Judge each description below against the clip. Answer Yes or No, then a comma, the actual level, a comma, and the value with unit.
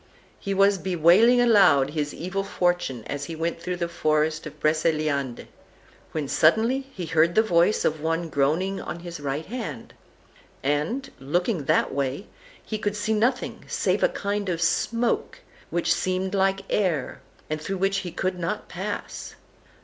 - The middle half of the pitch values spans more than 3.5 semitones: Yes, average, 4.3 semitones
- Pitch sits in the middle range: Yes, medium, 175 Hz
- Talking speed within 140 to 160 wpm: Yes, average, 155 wpm